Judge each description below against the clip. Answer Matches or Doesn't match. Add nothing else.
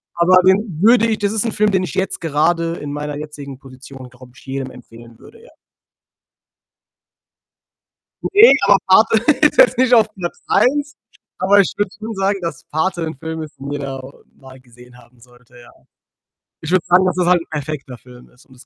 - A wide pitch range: Matches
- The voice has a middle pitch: Matches